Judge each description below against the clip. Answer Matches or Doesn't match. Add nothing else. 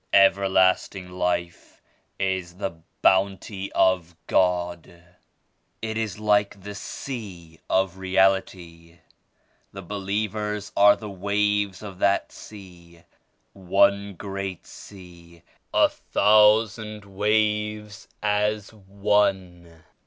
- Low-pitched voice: Matches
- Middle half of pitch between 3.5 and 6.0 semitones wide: Doesn't match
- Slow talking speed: Matches